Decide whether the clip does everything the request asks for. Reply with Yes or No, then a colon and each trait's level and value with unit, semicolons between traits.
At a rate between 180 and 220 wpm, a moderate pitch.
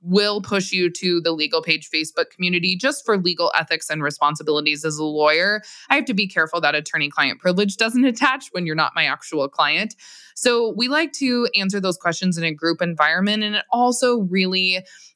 Yes: average, 200 wpm; medium, 180 Hz